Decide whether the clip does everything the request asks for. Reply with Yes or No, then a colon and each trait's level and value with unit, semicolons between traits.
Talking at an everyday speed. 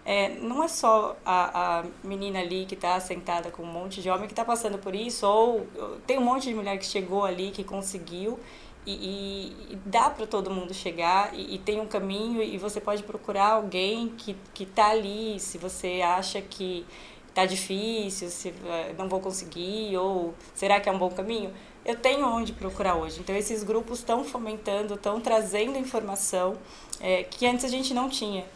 No: fast, 195 wpm